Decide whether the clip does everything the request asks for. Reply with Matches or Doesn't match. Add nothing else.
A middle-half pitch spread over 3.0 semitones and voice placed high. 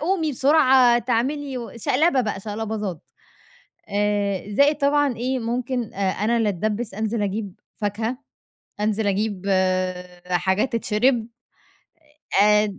Matches